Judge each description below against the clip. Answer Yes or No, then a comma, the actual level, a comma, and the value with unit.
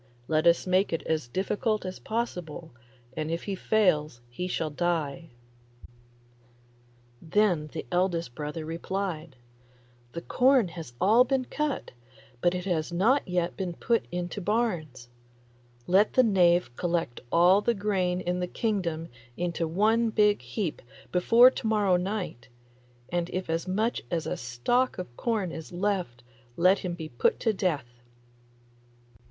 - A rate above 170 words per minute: No, average, 145 wpm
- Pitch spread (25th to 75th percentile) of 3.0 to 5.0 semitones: Yes, average, 4.1 semitones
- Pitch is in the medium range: Yes, medium, 180 Hz